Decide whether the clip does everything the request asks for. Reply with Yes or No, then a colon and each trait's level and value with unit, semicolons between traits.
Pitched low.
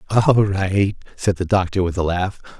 Yes: very low, 95 Hz